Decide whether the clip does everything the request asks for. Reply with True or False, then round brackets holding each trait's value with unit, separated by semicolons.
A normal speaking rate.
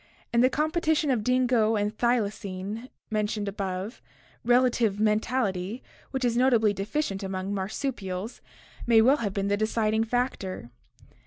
False (130 wpm)